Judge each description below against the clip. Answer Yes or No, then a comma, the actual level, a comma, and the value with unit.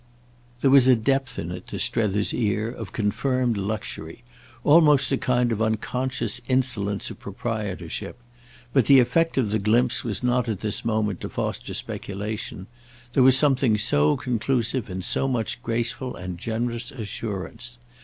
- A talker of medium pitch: No, low, 115 Hz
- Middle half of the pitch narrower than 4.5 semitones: Yes, average, 3.4 semitones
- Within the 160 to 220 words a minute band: No, average, 150 wpm